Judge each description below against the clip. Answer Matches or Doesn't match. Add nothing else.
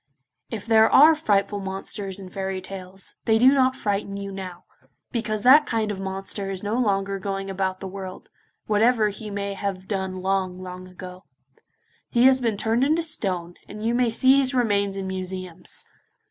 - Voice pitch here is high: Matches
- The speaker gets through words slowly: Doesn't match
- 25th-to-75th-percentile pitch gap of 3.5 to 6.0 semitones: Doesn't match